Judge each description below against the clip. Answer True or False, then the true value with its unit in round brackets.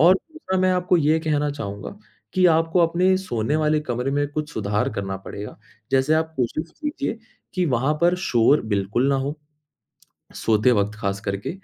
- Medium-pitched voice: True (145 Hz)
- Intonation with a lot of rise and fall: True (7.4 semitones)